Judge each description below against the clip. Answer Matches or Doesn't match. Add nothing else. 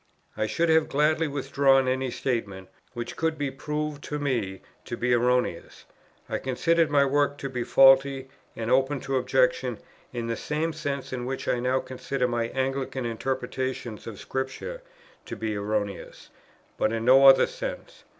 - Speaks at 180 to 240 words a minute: Doesn't match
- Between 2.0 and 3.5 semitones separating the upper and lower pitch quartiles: Matches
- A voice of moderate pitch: Doesn't match